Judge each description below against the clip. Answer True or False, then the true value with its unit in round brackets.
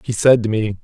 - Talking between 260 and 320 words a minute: True (290 wpm)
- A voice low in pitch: True (115 Hz)